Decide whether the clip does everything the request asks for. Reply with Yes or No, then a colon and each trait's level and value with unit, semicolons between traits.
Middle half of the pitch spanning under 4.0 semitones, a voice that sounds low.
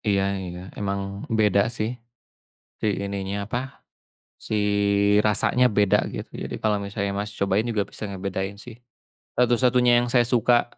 Yes: average, 3.3 semitones; low, 105 Hz